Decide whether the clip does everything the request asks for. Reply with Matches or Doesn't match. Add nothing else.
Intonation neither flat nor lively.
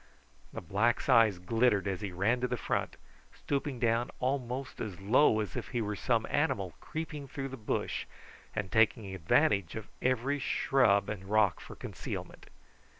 Matches